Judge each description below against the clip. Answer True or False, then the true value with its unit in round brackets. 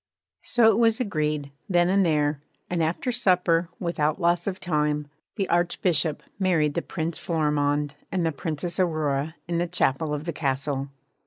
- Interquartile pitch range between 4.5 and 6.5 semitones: False (3.2 semitones)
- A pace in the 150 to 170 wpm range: True (160 wpm)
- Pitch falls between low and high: True (165 Hz)